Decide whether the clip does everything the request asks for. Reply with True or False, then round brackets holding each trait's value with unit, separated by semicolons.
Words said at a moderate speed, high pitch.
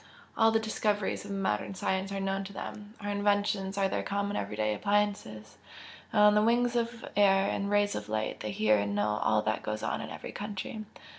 False (210 wpm; 200 Hz)